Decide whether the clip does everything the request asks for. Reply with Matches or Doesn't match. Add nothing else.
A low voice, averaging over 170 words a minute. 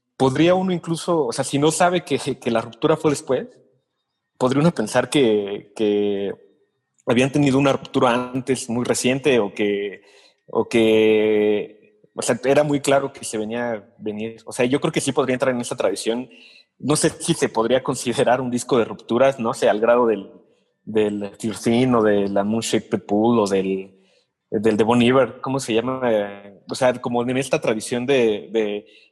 Matches